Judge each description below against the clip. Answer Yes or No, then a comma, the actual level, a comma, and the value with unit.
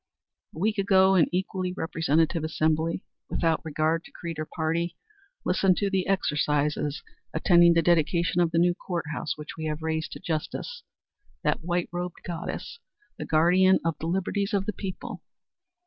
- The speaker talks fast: No, average, 165 wpm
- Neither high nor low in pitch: Yes, medium, 170 Hz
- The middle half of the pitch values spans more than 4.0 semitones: No, average, 2.7 semitones